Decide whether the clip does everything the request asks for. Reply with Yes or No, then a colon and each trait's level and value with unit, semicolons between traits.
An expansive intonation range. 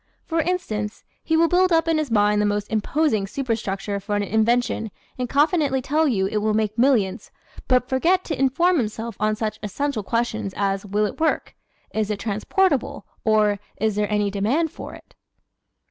Yes: wide, 5.7 semitones